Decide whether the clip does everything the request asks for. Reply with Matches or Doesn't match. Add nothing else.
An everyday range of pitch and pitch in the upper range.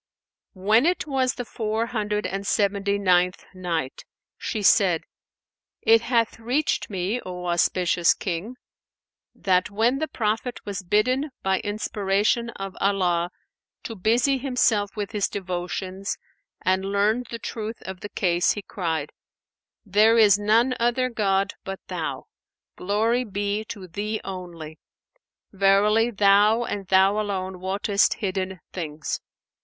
Matches